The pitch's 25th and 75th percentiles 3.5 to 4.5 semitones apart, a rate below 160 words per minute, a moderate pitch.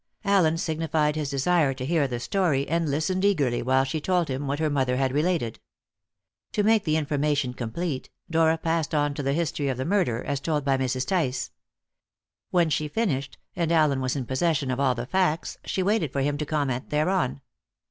No: average, 3.9 semitones; average, 195 wpm; medium, 150 Hz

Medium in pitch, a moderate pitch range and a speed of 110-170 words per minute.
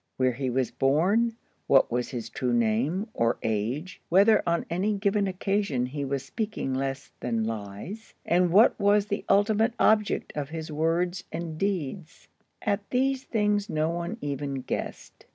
No: medium, 165 Hz; wide, 7.4 semitones; average, 150 wpm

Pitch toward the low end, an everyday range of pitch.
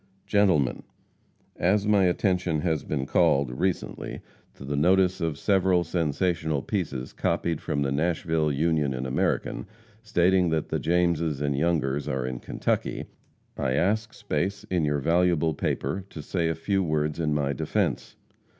Yes: very low, 80 Hz; average, 3.8 semitones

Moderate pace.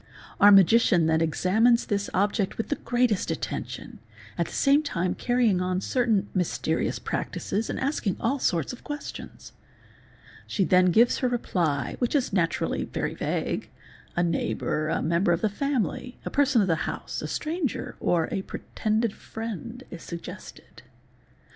Yes: average, 160 wpm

